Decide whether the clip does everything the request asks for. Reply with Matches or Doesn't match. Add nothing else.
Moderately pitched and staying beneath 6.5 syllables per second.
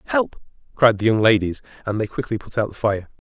Doesn't match